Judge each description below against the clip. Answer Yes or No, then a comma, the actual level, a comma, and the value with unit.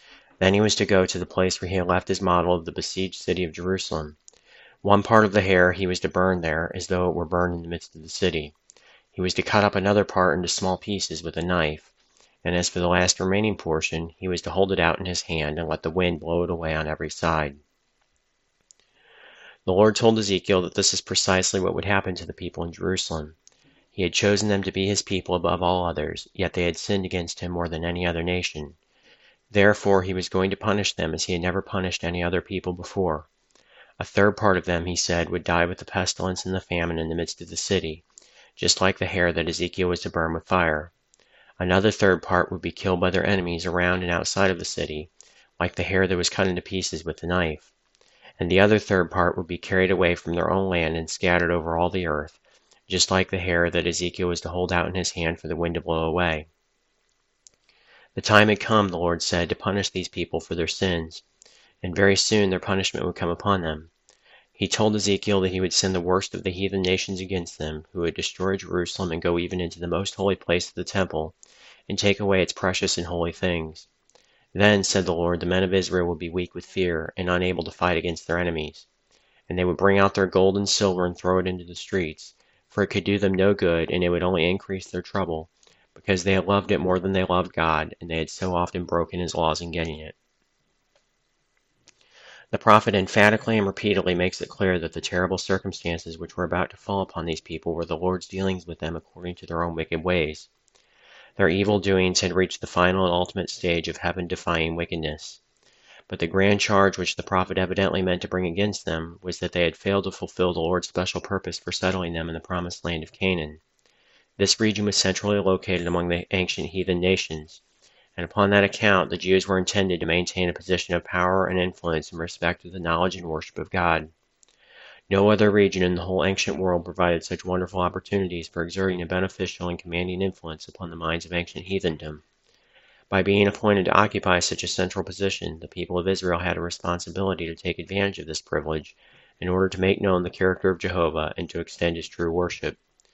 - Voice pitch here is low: Yes, very low, 90 Hz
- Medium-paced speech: No, fast, 225 wpm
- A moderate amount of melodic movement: No, narrow, 2.0 semitones